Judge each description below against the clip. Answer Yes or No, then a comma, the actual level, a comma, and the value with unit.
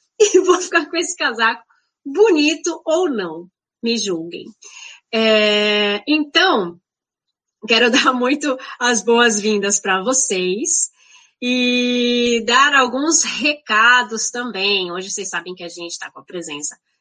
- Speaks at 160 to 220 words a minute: No, average, 125 wpm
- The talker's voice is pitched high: Yes, high, 245 Hz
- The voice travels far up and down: Yes, wide, 6.6 semitones